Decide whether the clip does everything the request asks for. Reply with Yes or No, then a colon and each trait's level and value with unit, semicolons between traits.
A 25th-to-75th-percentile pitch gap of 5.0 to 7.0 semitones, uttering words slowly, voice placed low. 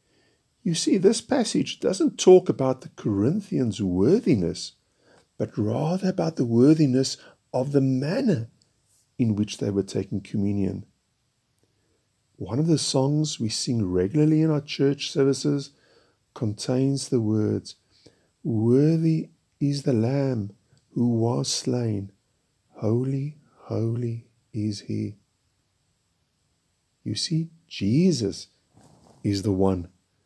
Yes: average, 5.3 semitones; slow, 110 wpm; low, 120 Hz